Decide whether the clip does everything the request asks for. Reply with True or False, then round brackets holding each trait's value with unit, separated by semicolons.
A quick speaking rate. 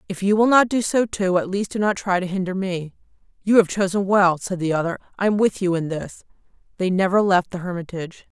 True (235 wpm)